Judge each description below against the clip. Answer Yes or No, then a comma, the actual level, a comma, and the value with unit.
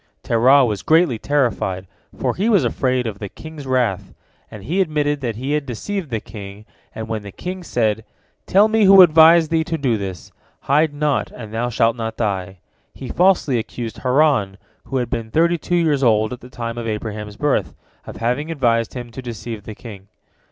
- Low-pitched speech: Yes, low, 125 Hz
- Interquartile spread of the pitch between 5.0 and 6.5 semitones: Yes, wide, 5.5 semitones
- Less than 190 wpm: No, average, 195 wpm